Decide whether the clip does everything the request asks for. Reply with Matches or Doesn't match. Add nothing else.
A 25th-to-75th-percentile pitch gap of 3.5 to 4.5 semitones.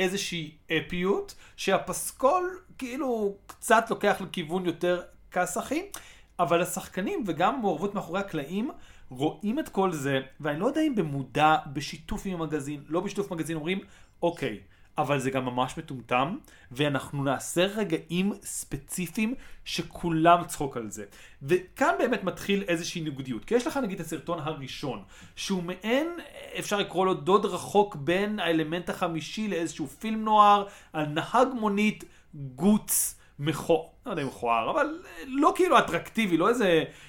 Doesn't match